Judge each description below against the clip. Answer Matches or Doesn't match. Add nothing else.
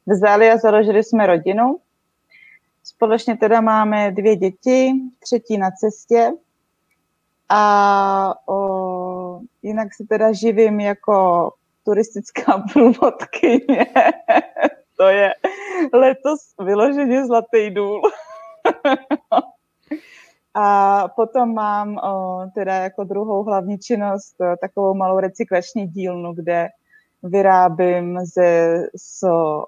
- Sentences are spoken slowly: Matches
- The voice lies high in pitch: Matches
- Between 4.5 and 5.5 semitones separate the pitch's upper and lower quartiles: Doesn't match